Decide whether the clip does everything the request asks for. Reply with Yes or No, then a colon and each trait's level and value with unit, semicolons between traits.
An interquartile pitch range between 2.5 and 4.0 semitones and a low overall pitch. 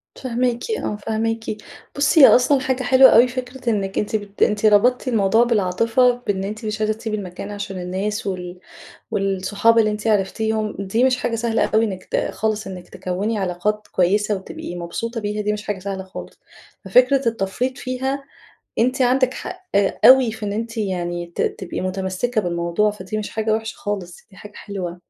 No: average, 3.5 semitones; high, 210 Hz